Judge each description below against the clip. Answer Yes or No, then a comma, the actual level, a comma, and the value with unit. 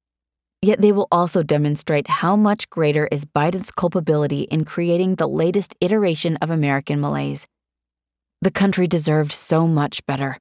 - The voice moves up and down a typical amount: Yes, average, 3.9 semitones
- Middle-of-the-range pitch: Yes, medium, 155 Hz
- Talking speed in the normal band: Yes, average, 145 wpm